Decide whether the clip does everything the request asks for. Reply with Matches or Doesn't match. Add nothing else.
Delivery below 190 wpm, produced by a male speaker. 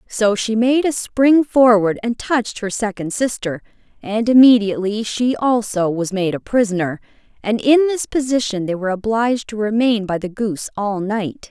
Doesn't match